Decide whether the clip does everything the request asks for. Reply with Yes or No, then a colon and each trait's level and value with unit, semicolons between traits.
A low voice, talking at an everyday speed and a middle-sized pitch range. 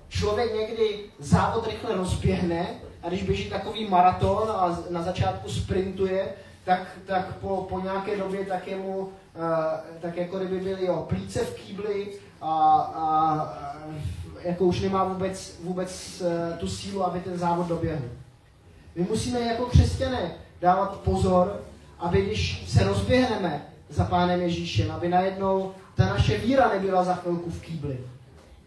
No: medium, 180 Hz; average, 145 wpm; average, 3.1 semitones